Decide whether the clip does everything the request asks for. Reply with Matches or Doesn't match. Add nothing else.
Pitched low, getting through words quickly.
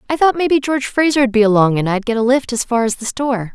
Doesn't match